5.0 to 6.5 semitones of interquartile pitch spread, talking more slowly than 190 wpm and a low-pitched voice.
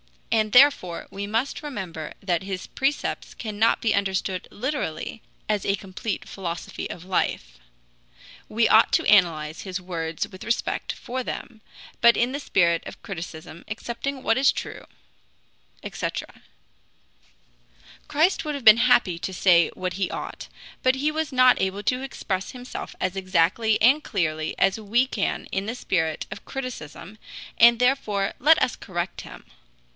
No: average, 5.3 semitones; average, 150 wpm; high, 205 Hz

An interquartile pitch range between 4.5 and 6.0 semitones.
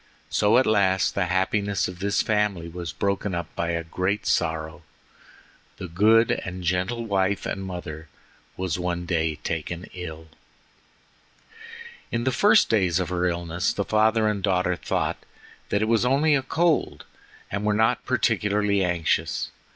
No: average, 3.3 semitones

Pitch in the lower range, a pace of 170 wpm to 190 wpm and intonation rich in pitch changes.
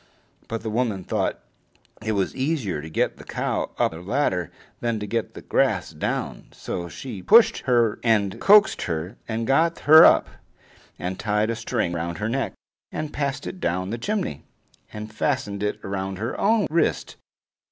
Yes: low, 110 Hz; average, 175 wpm; wide, 5.9 semitones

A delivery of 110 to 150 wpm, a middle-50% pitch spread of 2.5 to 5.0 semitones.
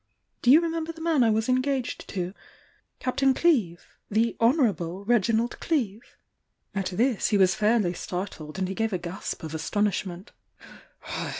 No: average, 145 wpm; wide, 5.5 semitones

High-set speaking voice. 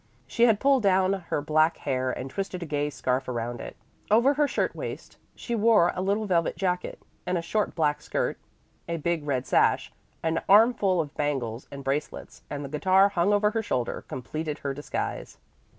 No: medium, 170 Hz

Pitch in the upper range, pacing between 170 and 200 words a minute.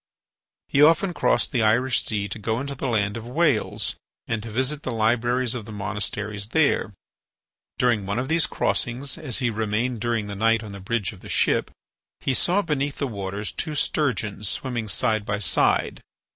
No: low, 115 Hz; average, 185 wpm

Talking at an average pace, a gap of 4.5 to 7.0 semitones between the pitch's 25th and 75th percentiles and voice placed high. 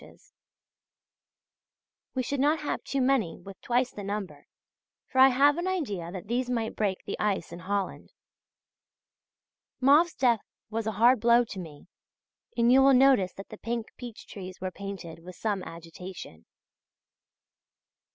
Yes: average, 150 wpm; wide, 5.6 semitones; high, 220 Hz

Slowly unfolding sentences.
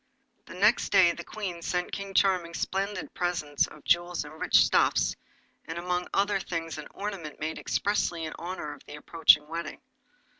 No: average, 165 wpm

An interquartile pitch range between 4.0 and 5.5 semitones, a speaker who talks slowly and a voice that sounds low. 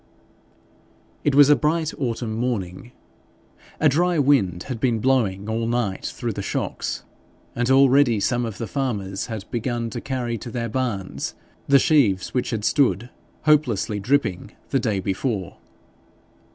No: average, 4.3 semitones; average, 145 wpm; low, 120 Hz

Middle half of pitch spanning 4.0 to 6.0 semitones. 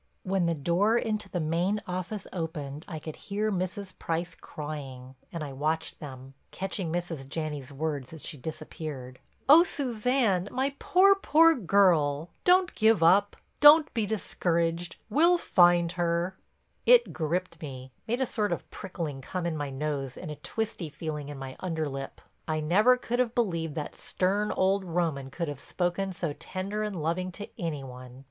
Yes: average, 5.2 semitones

